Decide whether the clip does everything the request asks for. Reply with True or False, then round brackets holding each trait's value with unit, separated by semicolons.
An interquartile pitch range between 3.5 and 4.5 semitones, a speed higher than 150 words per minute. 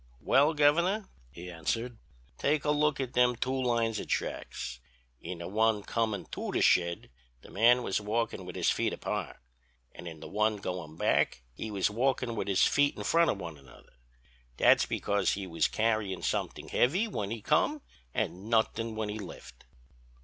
False (4.9 semitones; 180 wpm)